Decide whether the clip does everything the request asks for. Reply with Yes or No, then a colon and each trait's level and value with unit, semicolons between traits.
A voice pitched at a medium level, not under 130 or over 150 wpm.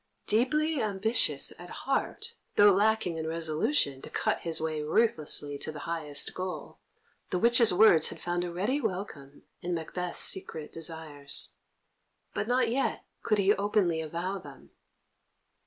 Yes: medium, 180 Hz; average, 140 wpm